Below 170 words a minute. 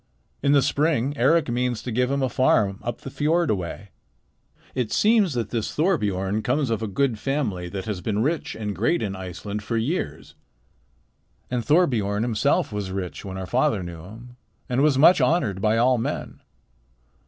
No: average, 180 wpm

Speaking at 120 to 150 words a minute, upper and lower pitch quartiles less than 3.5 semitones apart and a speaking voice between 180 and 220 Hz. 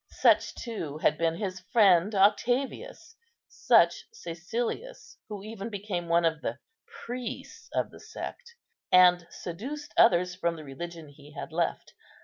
No: slow, 135 wpm; average, 5.3 semitones; medium, 185 Hz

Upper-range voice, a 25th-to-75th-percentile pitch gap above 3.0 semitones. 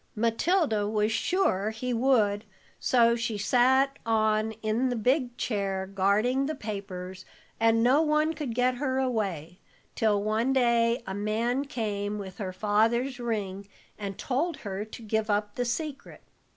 Yes: high, 225 Hz; average, 3.6 semitones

